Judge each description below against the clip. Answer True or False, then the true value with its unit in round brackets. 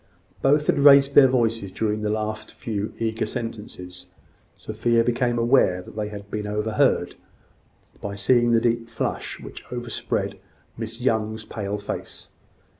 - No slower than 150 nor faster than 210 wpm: False (140 wpm)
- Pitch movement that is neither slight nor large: False (2.2 semitones)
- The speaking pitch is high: False (110 Hz)